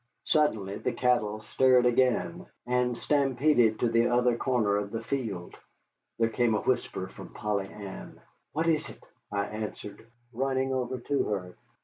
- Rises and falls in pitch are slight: No, average, 3.7 semitones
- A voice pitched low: Yes, low, 120 Hz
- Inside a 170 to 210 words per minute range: No, average, 150 wpm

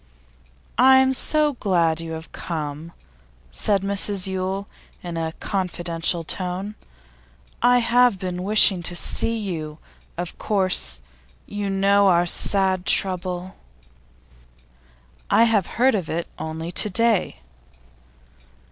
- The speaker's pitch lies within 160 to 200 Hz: Yes, medium, 185 Hz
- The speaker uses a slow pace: Yes, slow, 115 wpm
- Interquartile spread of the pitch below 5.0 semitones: Yes, average, 3.2 semitones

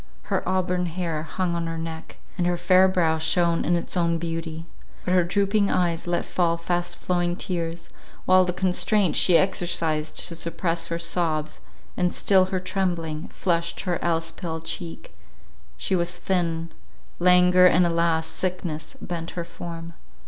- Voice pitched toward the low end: No, medium, 170 Hz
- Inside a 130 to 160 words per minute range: Yes, average, 155 wpm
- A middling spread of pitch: No, narrow, 1.6 semitones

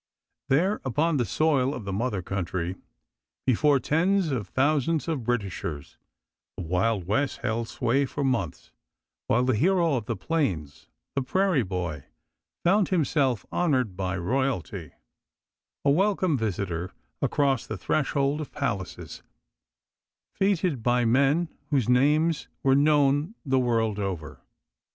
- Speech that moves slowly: Yes, slow, 130 wpm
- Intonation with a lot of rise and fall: Yes, wide, 6.9 semitones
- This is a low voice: Yes, low, 130 Hz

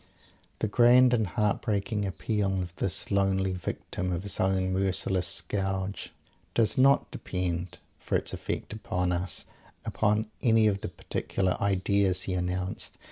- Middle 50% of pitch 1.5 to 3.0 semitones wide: Yes, narrow, 2.4 semitones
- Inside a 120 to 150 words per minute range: Yes, average, 140 wpm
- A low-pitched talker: Yes, very low, 95 Hz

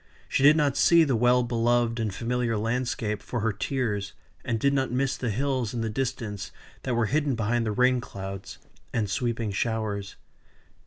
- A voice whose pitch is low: Yes, low, 120 Hz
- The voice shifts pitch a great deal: No, average, 2.9 semitones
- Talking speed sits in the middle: Yes, average, 175 wpm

